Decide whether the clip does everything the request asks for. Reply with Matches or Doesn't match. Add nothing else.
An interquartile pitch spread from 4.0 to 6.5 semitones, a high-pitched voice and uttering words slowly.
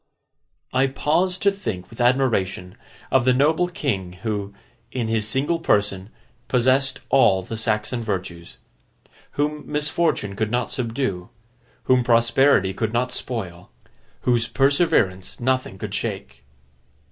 Doesn't match